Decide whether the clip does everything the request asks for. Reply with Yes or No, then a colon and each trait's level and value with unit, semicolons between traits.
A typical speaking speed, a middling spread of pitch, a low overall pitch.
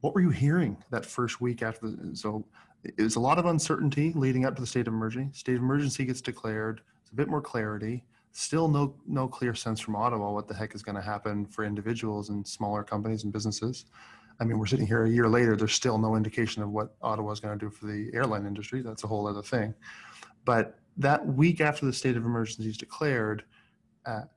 No: fast, 230 wpm; average, 3.3 semitones; low, 110 Hz